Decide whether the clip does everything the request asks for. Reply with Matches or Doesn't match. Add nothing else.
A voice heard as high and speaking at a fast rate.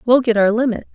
Matches